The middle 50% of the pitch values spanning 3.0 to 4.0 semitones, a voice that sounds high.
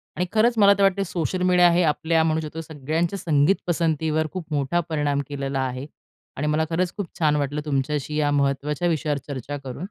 No: average, 3.3 semitones; medium, 155 Hz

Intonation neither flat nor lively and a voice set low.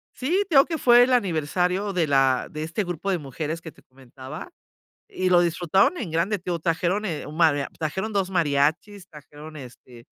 No: average, 4.8 semitones; medium, 170 Hz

